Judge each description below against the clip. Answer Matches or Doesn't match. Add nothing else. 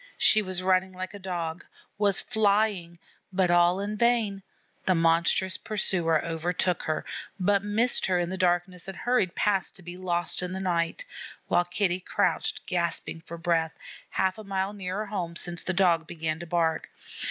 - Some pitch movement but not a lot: Doesn't match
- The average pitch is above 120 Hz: Matches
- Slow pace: Doesn't match